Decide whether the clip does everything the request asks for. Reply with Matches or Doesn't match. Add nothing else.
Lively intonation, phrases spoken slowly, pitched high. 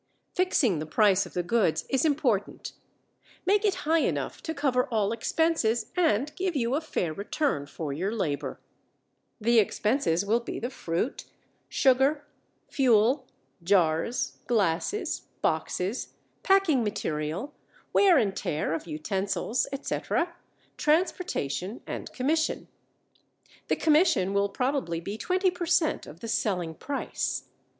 Matches